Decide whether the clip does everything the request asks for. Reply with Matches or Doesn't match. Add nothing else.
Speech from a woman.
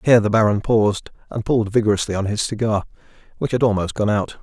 Doesn't match